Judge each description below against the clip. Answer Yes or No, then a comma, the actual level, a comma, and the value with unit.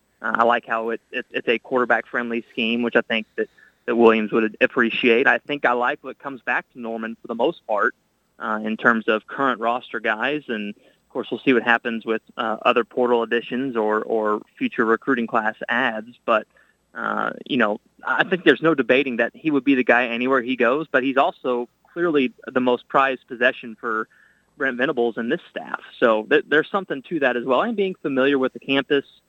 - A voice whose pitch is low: Yes, low, 120 Hz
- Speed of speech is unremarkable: No, fast, 210 wpm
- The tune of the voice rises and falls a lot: No, average, 2.7 semitones